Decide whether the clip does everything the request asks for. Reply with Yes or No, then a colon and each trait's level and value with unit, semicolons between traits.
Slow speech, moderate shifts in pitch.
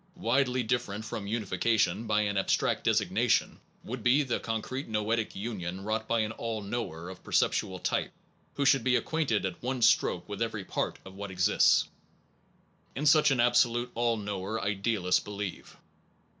No: average, 165 wpm; average, 3.1 semitones